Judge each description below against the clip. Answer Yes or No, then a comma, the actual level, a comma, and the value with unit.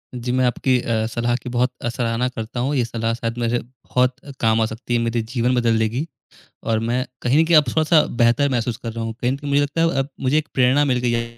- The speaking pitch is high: No, low, 120 Hz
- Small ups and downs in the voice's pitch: Yes, narrow, 2.2 semitones